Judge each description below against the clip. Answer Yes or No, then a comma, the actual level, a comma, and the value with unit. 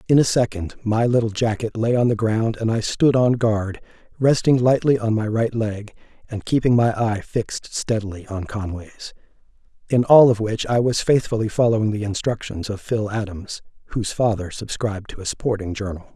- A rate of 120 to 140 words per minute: No, average, 180 wpm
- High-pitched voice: No, low, 110 Hz